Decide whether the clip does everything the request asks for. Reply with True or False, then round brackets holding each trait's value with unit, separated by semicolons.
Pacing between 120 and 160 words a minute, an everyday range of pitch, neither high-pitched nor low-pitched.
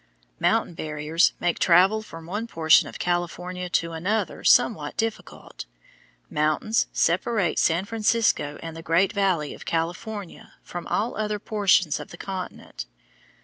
True (135 wpm; 4.2 semitones; 180 Hz)